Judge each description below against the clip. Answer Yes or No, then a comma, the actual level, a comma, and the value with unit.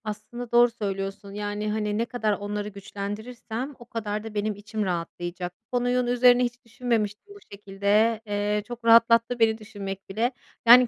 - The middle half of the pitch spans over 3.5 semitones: No, average, 2.7 semitones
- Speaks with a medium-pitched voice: No, high, 215 Hz